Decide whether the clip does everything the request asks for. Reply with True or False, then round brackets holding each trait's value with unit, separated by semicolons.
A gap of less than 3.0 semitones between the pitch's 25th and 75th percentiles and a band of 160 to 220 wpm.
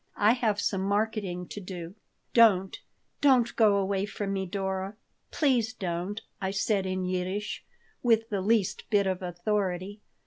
False (2.4 semitones; 145 wpm)